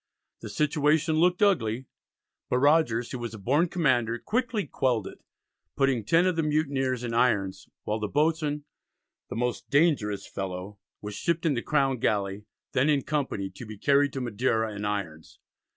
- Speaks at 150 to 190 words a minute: Yes, average, 170 wpm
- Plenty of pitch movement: Yes, wide, 5.9 semitones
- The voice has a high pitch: No, low, 130 Hz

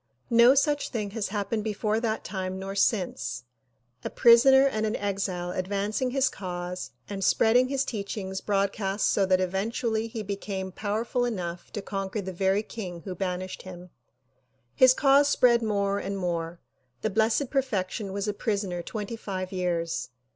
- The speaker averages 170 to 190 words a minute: No, average, 155 wpm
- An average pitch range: Yes, average, 3.3 semitones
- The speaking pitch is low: No, high, 200 Hz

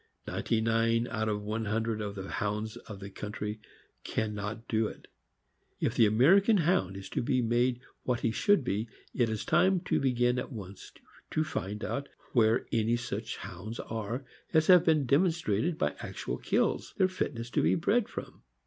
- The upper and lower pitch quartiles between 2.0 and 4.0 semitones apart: No, average, 4.4 semitones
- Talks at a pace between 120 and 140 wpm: No, average, 180 wpm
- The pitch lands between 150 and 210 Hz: No, low, 115 Hz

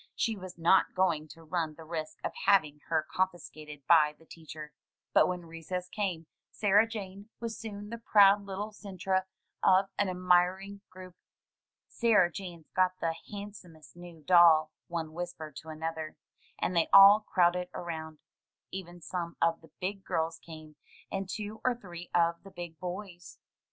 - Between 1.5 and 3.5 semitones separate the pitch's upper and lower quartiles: Yes, average, 3.1 semitones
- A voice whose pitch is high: No, medium, 175 Hz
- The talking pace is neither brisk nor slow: Yes, average, 155 wpm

